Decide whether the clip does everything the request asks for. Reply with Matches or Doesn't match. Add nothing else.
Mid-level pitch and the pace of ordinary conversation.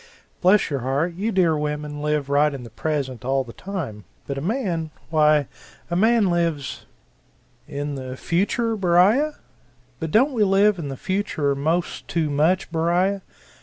Matches